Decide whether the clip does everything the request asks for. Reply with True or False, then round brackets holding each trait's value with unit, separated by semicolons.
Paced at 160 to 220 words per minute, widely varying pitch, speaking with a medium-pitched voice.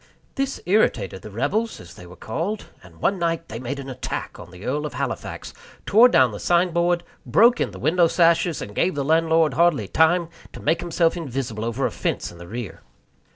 True (200 wpm; 6.8 semitones; 160 Hz)